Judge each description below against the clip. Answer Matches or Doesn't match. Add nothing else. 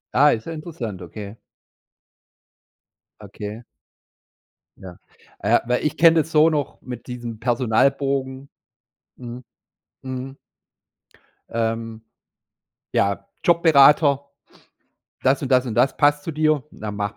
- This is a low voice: Matches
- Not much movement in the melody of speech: Doesn't match